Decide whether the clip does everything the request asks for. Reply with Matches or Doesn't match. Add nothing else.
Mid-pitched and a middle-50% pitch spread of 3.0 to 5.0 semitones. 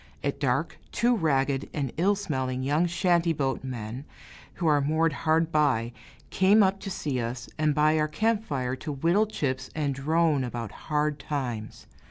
Matches